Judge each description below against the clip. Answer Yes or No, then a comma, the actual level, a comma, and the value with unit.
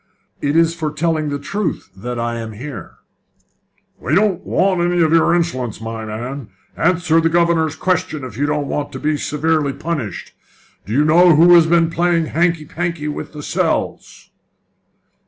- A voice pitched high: No, medium, 155 Hz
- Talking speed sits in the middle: Yes, average, 170 wpm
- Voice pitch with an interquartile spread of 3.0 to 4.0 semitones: Yes, average, 3.3 semitones